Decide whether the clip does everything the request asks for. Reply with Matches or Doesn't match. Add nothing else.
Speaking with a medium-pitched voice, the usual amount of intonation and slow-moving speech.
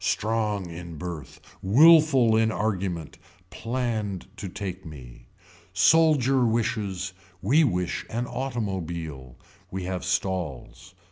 Doesn't match